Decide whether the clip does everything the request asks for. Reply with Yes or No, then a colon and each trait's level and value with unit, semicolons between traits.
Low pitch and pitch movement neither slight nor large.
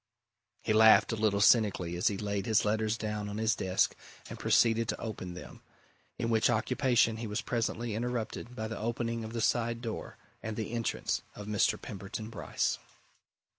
No: low, 110 Hz; narrow, 1.8 semitones